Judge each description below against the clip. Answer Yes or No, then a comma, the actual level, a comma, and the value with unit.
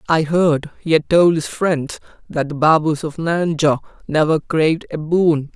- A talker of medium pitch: Yes, medium, 155 Hz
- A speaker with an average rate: Yes, average, 175 wpm